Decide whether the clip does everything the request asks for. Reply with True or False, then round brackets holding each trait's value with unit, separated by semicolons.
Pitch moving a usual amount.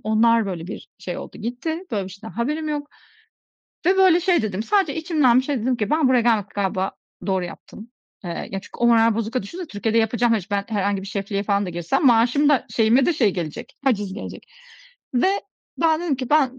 False (6.2 semitones)